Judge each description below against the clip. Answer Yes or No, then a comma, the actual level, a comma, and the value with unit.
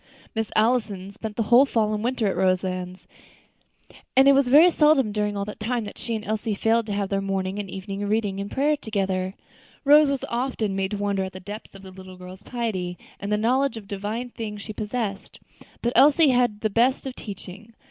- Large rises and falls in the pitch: No, average, 3.5 semitones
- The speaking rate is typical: No, fast, 215 wpm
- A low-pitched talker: No, high, 210 Hz